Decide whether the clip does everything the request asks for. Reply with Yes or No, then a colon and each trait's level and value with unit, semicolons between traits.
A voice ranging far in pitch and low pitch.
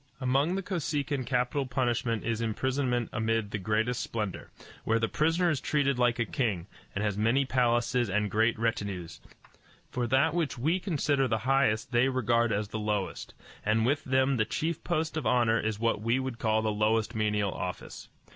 No: average, 3.7 semitones; low, 120 Hz